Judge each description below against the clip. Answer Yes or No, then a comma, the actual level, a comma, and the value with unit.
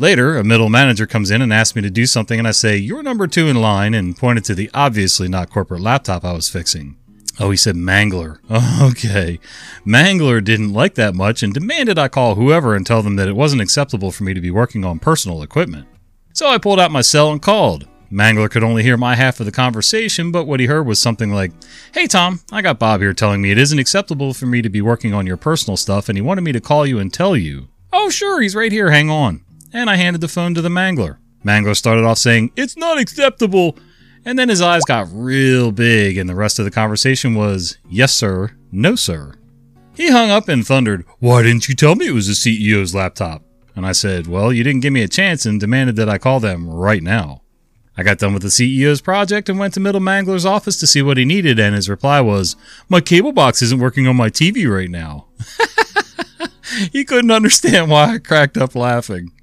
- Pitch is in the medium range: No, low, 120 Hz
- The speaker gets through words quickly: Yes, fast, 230 wpm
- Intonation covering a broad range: Yes, wide, 7.2 semitones